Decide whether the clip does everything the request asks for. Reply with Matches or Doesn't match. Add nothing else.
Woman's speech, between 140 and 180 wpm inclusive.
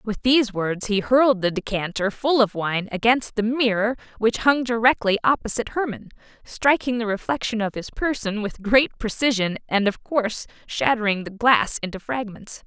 Matches